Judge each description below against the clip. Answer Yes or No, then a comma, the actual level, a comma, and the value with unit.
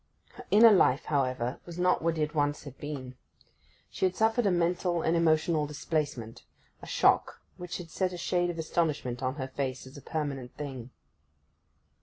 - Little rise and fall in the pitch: No, average, 4.4 semitones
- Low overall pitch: No, medium, 155 Hz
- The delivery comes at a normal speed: Yes, average, 170 wpm